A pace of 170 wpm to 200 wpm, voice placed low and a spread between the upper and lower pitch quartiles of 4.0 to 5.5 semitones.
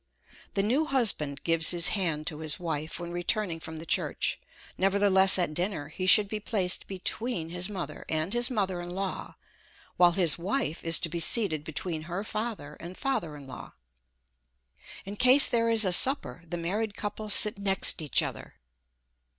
No: average, 175 wpm; medium, 185 Hz; average, 4.3 semitones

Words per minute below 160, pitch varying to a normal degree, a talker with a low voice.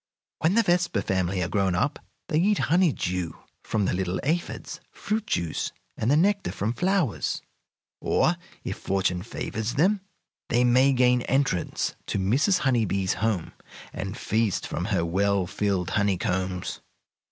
No: average, 150 wpm; wide, 7.9 semitones; low, 110 Hz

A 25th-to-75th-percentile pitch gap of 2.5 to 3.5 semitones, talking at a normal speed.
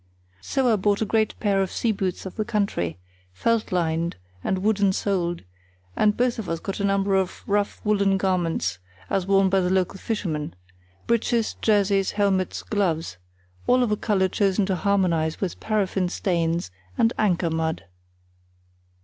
Yes: average, 2.8 semitones; average, 160 wpm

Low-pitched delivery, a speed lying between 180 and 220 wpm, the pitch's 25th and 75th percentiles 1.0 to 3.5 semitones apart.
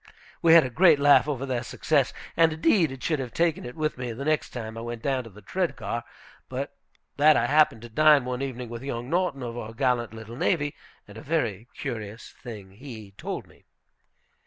No: low, 130 Hz; fast, 205 wpm; average, 4.7 semitones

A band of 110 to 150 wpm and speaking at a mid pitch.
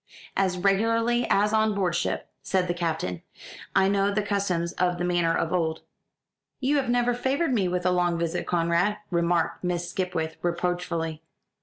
No: average, 165 wpm; medium, 180 Hz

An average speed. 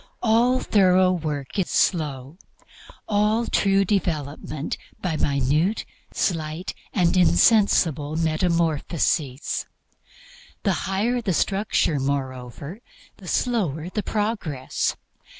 No: slow, 90 wpm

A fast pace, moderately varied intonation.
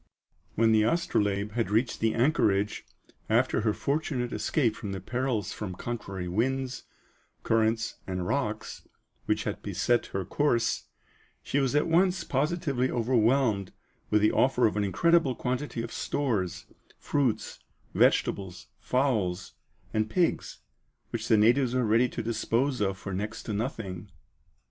No: average, 140 wpm; average, 4.1 semitones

